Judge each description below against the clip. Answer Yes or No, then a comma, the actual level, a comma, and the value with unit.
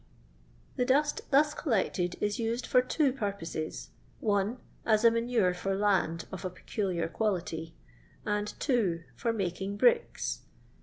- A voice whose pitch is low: No, high, 205 Hz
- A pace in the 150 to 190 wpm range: No, average, 140 wpm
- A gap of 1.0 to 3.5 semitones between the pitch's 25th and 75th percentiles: No, average, 4.8 semitones